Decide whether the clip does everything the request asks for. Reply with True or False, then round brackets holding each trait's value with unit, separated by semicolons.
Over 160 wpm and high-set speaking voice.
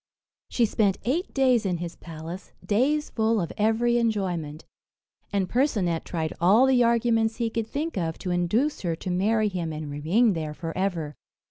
True (170 wpm; 200 Hz)